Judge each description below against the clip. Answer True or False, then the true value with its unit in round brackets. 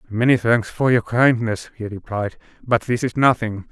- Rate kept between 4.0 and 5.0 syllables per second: True (4.6 syllables/s)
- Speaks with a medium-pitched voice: False (115 Hz)